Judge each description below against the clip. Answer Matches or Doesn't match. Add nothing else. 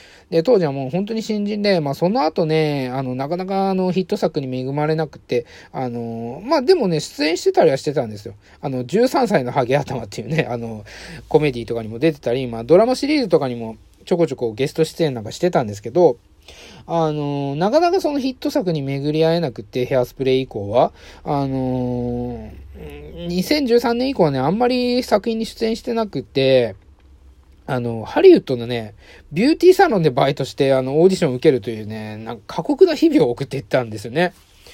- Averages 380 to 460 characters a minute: Matches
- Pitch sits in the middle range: Matches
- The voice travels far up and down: Matches